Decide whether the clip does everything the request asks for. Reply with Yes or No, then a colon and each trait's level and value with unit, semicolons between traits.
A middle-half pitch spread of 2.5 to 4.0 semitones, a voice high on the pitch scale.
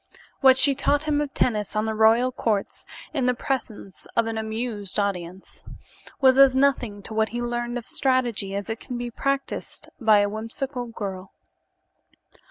Yes: average, 3.5 semitones; high, 235 Hz